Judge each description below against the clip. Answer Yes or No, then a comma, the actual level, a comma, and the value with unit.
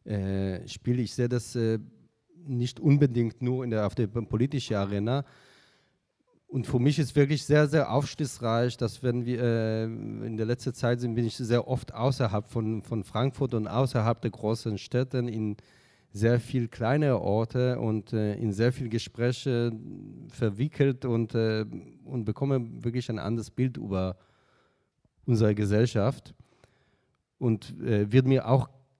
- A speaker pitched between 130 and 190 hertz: No, low, 120 Hz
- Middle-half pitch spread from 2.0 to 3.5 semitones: Yes, average, 2.7 semitones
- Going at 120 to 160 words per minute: Yes, average, 150 wpm